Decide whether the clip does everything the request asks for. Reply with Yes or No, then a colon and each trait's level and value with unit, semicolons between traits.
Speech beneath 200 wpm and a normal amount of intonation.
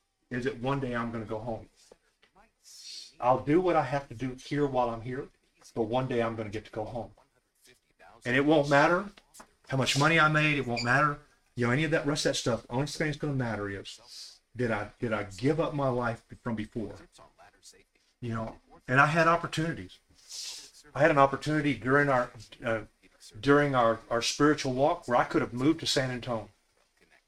No: fast, 205 wpm; average, 4.1 semitones